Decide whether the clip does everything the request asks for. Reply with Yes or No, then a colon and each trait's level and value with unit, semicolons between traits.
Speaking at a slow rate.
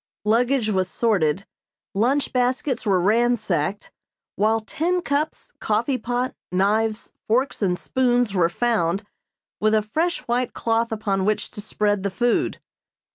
Yes: slow, 130 wpm